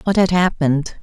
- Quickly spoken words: No, average, 175 wpm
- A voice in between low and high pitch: Yes, medium, 170 Hz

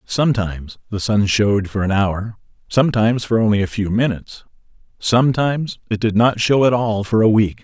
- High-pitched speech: No, low, 110 Hz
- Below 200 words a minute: Yes, average, 180 wpm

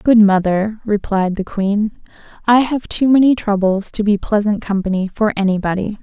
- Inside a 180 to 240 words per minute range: No, average, 160 wpm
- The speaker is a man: No, female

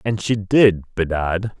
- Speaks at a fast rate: No, average, 150 wpm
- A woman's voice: No, male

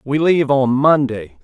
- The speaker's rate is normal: Yes, average, 170 wpm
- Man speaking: Yes, male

